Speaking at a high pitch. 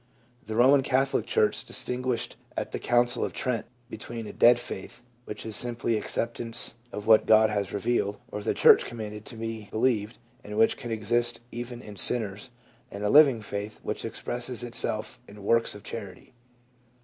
No: low, 115 Hz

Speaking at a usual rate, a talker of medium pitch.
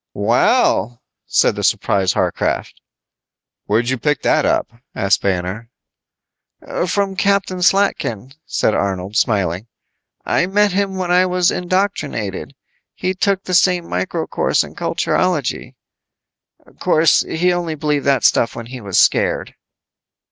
No: slow, 125 wpm; medium, 150 Hz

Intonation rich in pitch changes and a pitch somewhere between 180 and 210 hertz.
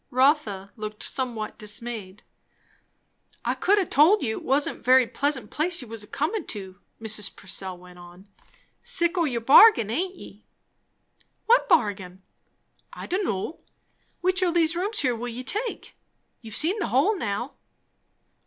No: wide, 8.5 semitones; very high, 255 Hz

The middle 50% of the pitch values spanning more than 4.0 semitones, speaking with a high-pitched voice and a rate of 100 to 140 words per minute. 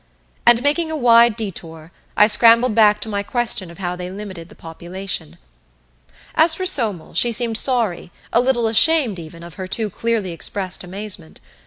No: average, 4.8 semitones; high, 210 Hz; average, 170 wpm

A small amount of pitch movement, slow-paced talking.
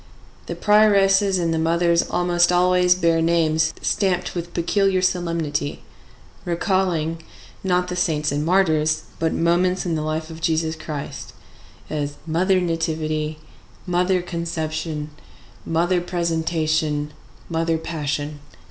Yes: narrow, 2.2 semitones; slow, 115 wpm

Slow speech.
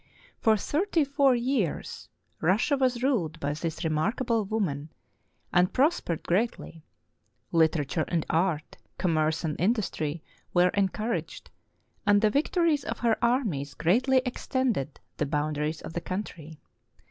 Yes: slow, 125 wpm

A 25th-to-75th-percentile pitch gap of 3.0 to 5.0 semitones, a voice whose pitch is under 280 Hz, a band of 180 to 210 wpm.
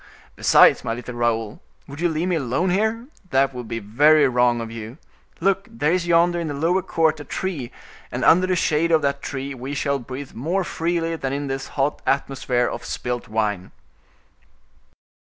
No: wide, 5.4 semitones; medium, 140 Hz; average, 185 wpm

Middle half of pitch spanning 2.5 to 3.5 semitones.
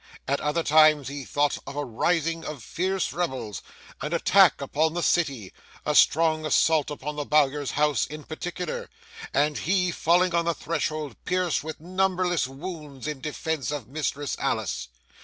Yes: average, 2.9 semitones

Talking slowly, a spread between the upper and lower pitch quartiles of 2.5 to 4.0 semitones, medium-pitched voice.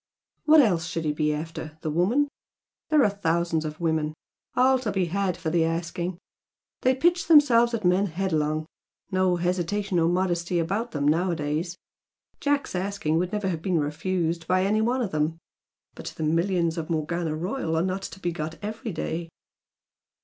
No: average, 170 wpm; average, 3.6 semitones; medium, 175 Hz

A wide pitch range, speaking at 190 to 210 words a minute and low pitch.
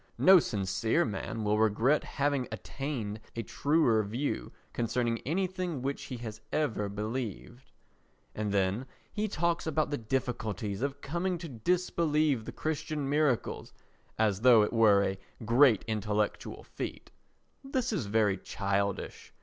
No: wide, 6.1 semitones; slow, 135 wpm; low, 120 Hz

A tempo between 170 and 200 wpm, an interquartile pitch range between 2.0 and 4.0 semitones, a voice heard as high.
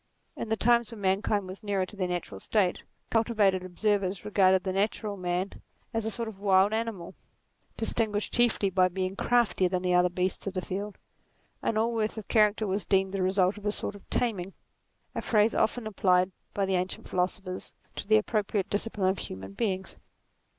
Yes: average, 190 wpm; narrow, 2.6 semitones; high, 195 Hz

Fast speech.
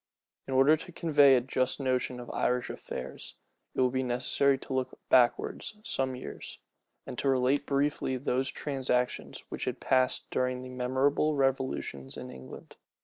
No: average, 155 wpm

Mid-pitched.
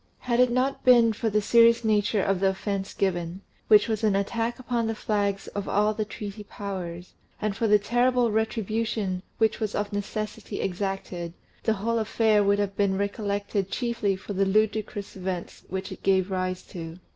No: high, 205 Hz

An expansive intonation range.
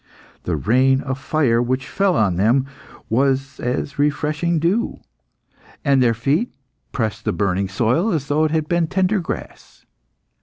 No: average, 4.9 semitones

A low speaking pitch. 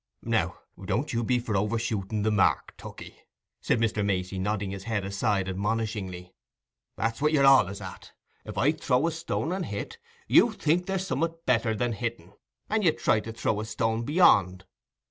Yes: low, 115 Hz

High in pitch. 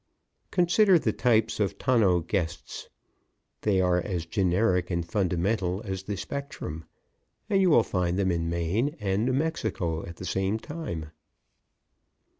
No: very low, 95 Hz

